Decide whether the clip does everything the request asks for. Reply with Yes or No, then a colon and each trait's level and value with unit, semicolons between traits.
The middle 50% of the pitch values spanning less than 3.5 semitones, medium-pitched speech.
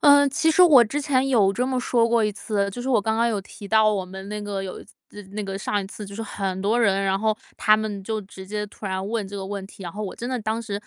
No: average, 3.0 semitones; high, 210 Hz